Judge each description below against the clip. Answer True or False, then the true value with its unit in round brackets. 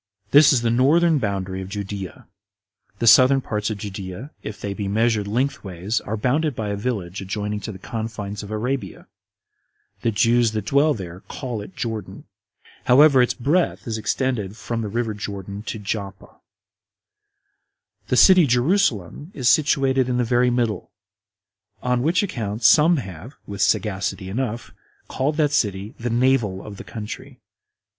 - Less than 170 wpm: True (155 wpm)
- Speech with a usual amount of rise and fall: True (4.3 semitones)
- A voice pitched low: True (115 Hz)